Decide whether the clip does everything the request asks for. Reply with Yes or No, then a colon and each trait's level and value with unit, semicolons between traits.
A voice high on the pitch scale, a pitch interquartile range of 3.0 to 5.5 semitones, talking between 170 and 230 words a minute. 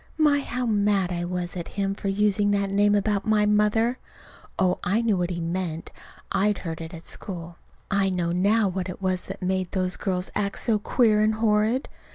No: high, 195 Hz; narrow, 2.6 semitones; average, 200 wpm